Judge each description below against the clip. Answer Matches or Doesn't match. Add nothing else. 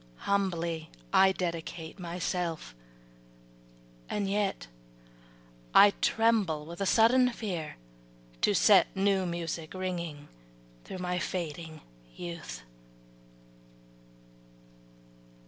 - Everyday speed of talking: Doesn't match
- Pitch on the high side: Doesn't match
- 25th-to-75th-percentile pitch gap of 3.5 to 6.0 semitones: Doesn't match